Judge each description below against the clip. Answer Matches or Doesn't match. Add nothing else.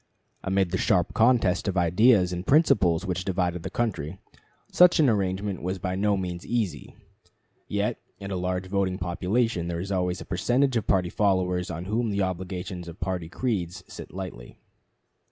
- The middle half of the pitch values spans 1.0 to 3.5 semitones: Matches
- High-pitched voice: Doesn't match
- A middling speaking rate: Matches